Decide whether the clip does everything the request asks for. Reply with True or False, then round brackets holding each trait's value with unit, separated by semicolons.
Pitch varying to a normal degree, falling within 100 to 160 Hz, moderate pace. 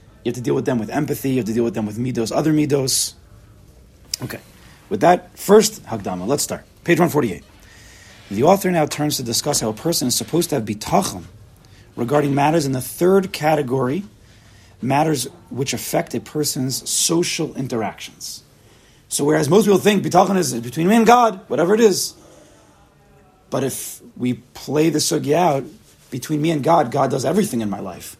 False (6.3 semitones; 140 Hz; 180 wpm)